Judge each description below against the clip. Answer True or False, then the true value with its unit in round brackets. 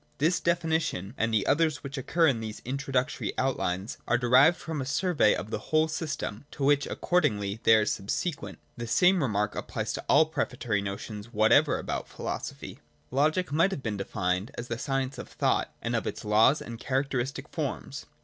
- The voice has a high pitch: False (130 Hz)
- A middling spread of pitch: False (6.2 semitones)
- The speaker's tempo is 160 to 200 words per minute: True (180 wpm)